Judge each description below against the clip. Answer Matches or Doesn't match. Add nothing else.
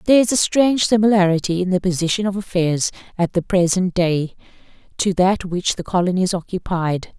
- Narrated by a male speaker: Doesn't match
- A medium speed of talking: Matches